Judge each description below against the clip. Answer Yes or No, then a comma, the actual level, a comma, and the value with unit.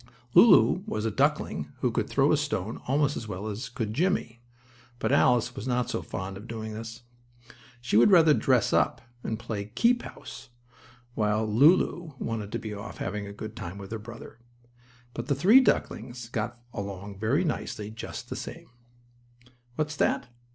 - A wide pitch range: No, average, 4.1 semitones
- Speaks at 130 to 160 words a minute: No, average, 175 wpm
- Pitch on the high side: No, low, 115 Hz